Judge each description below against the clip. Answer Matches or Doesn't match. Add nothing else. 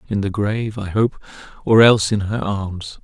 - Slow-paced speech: Doesn't match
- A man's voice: Matches